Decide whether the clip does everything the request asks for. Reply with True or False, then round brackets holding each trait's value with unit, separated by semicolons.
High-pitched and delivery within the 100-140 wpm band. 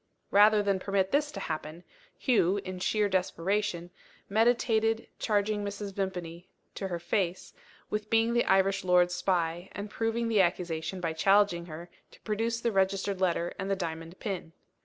False (195 Hz; 160 wpm)